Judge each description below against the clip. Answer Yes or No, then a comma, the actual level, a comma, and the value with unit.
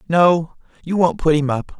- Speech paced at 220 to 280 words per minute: No, average, 200 wpm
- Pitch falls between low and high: Yes, medium, 165 Hz